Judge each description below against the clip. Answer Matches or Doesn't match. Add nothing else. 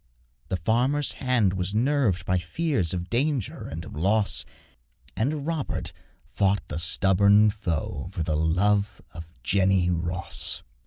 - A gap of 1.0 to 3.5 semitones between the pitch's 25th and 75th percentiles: Doesn't match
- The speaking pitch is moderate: Doesn't match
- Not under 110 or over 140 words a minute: Matches